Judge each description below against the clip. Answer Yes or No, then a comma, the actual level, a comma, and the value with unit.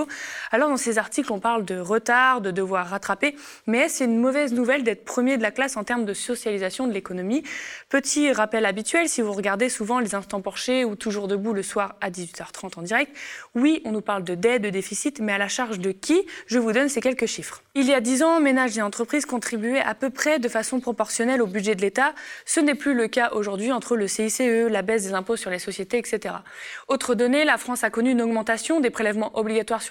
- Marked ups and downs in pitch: No, average, 3.8 semitones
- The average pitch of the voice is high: Yes, high, 230 Hz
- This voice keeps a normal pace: No, fast, 230 wpm